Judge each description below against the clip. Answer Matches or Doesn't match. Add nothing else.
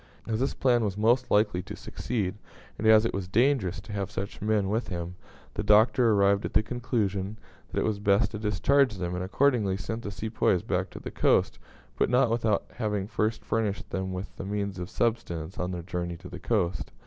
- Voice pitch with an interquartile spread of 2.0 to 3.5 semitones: Matches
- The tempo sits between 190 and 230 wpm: Matches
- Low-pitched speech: Matches